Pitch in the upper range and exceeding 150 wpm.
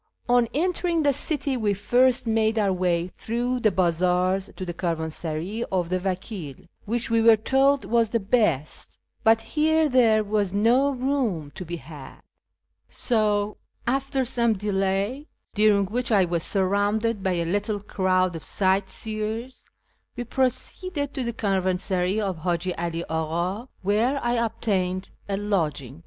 No: high, 205 Hz; average, 145 wpm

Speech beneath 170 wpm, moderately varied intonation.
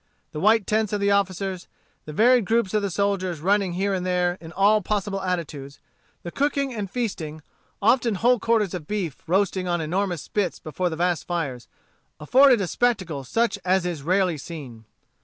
No: average, 175 wpm; average, 3.6 semitones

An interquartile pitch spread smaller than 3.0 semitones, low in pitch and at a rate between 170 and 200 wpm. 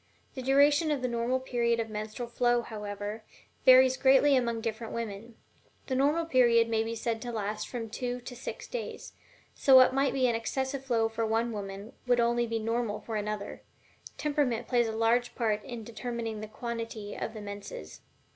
No: narrow, 2.5 semitones; high, 235 Hz; average, 185 wpm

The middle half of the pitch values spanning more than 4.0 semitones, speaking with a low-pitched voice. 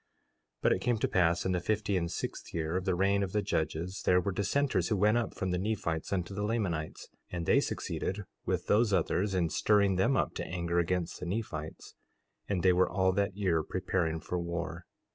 No: average, 2.8 semitones; very low, 95 Hz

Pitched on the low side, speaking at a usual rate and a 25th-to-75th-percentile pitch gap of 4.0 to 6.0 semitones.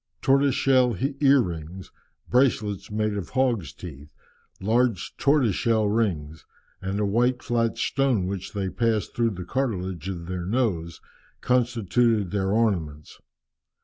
No: low, 105 Hz; slow, 130 wpm; average, 5.0 semitones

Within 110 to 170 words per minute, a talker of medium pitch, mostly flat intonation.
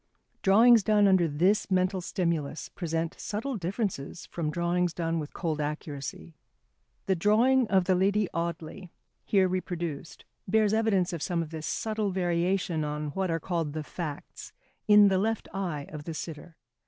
No: average, 155 wpm; medium, 175 Hz; average, 3.6 semitones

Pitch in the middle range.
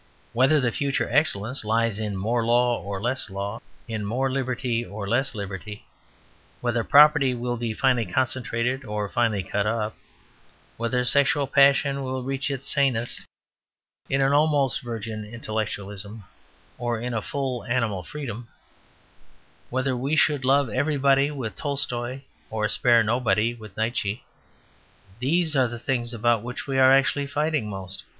No: low, 120 Hz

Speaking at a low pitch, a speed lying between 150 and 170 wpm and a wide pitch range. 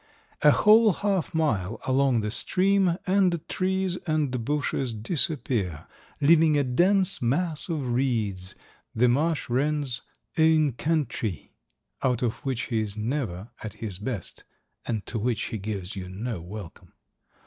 No: low, 130 Hz; slow, 135 wpm; wide, 6.6 semitones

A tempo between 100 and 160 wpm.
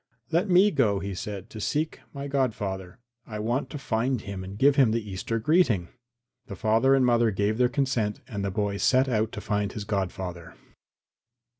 No: average, 185 wpm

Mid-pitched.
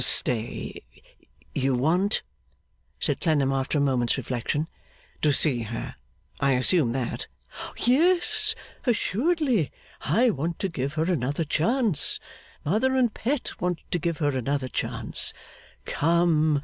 Yes: medium, 160 Hz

